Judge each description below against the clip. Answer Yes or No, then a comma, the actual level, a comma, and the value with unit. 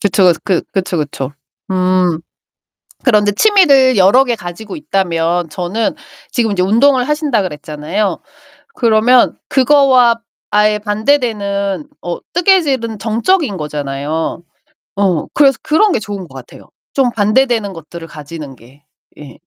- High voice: Yes, high, 205 Hz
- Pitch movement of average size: No, wide, 6.5 semitones